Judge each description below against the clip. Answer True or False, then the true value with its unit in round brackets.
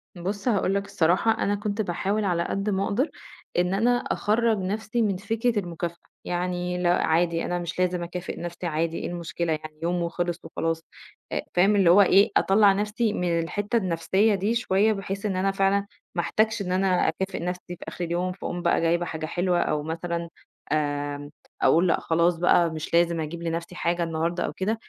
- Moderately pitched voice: True (180 Hz)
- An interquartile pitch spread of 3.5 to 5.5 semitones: False (2.9 semitones)